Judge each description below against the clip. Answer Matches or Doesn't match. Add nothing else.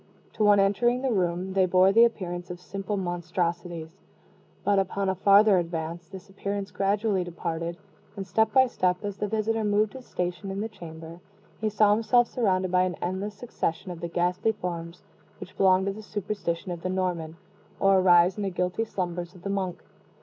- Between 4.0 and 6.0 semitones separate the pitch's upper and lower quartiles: Doesn't match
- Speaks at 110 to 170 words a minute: Doesn't match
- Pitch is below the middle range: Doesn't match